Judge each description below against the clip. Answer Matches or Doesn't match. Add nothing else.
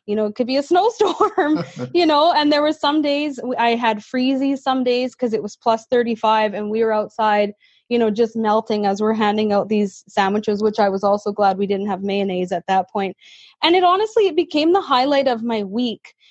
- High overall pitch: Matches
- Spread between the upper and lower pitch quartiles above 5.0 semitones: Matches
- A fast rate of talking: Matches